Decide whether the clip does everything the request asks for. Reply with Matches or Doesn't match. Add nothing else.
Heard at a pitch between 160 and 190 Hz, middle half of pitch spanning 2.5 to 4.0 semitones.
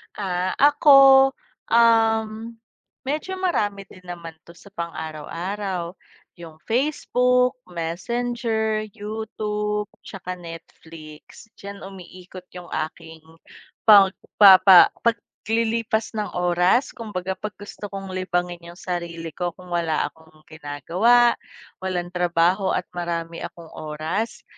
Doesn't match